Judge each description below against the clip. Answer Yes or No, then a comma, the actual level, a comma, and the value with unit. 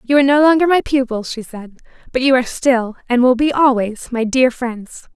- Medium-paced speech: No, fast, 220 wpm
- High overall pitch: Yes, very high, 250 Hz